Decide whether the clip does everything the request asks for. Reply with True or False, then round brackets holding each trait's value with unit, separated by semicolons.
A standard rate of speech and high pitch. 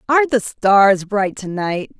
True (150 wpm; 210 Hz)